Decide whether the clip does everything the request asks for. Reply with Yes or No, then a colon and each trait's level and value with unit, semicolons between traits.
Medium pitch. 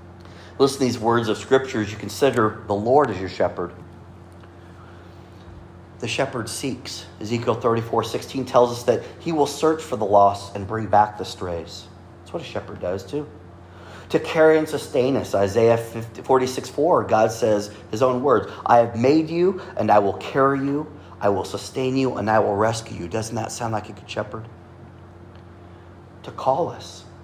No: low, 110 Hz